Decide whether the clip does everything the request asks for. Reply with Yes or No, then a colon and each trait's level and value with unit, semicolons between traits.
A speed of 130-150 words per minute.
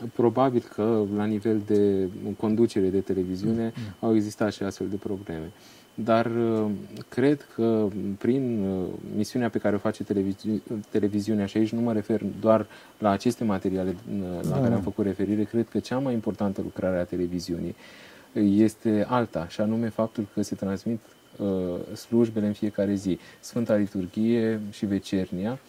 Yes: average, 145 wpm